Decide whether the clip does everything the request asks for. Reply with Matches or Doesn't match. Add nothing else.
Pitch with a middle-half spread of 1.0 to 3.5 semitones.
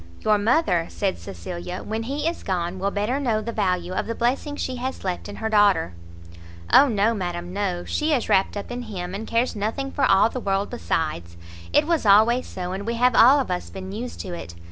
Doesn't match